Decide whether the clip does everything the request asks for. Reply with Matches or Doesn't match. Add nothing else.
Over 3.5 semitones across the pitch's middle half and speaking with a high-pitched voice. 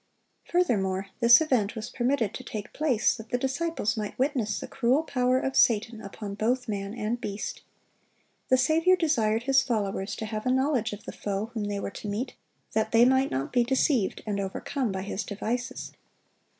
Matches